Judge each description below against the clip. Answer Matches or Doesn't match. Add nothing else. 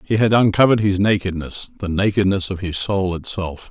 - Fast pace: Doesn't match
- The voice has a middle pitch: Doesn't match